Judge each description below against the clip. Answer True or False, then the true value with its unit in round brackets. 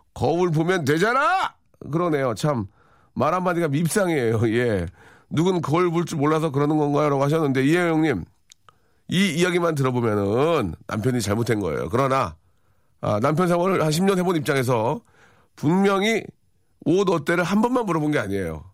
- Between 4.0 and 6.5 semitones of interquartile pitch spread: False (6.9 semitones)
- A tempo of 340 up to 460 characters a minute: False (330 characters per minute)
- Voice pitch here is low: False (150 Hz)